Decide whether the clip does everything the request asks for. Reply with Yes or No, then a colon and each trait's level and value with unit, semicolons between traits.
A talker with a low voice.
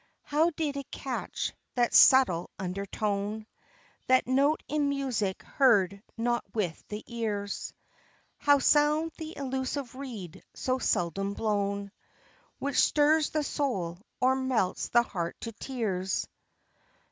No: high, 240 Hz